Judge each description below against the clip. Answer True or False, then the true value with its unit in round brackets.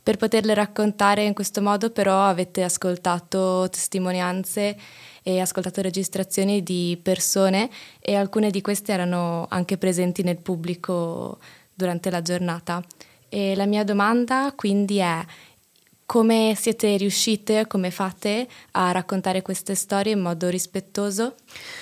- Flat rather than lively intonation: True (2.3 semitones)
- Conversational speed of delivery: True (125 wpm)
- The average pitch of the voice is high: True (195 Hz)